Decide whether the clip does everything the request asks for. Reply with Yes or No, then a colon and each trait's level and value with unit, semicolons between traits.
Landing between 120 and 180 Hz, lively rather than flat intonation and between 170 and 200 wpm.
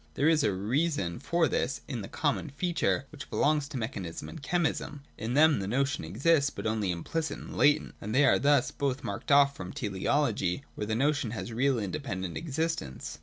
Yes: medium, 140 Hz; wide, 5.9 semitones; average, 190 wpm